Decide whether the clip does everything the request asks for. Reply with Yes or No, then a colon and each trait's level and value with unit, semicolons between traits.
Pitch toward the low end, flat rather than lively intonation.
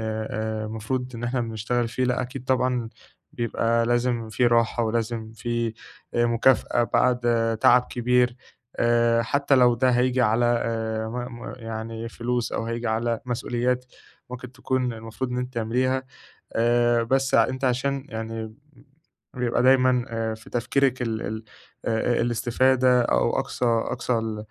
Yes: low, 120 Hz; narrow, 1.8 semitones